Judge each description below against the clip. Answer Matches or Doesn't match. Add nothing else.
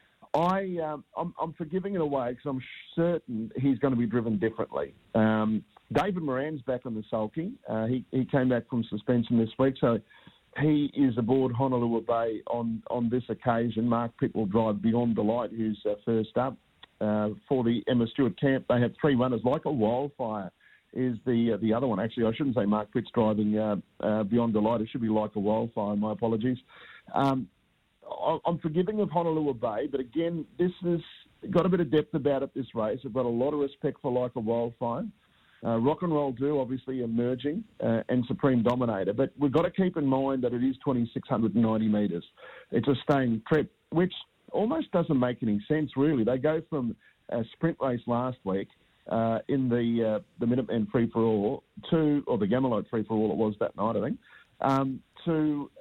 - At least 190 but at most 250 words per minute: Matches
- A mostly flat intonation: Doesn't match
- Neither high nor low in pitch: Doesn't match